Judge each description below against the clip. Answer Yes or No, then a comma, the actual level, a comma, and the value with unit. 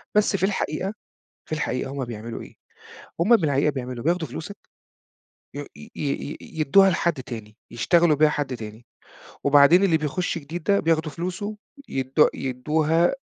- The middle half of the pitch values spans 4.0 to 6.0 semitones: Yes, average, 4.6 semitones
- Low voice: No, medium, 150 Hz